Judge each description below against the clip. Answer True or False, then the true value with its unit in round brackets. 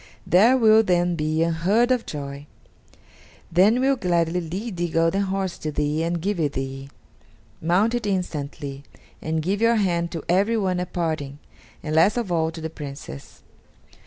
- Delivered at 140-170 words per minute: True (160 wpm)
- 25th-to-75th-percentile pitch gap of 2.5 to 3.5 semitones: False (4.1 semitones)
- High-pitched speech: False (170 Hz)